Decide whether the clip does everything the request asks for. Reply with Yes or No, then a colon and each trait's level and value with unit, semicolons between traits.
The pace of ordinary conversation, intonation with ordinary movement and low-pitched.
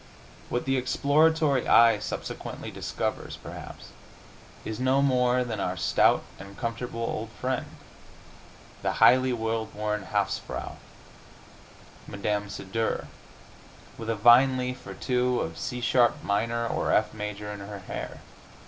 No: slow, 130 wpm; average, 3.2 semitones; low, 115 Hz